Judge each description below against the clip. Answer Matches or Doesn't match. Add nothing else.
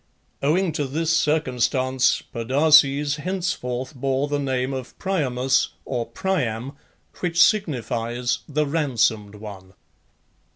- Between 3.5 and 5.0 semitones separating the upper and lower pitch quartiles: Matches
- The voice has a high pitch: Doesn't match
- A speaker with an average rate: Doesn't match